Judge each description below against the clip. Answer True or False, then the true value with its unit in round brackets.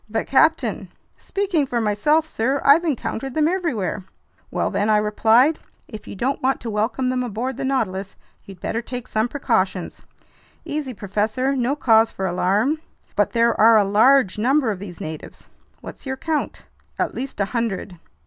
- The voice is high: True (235 Hz)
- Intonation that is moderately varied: True (4.6 semitones)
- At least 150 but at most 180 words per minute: True (170 wpm)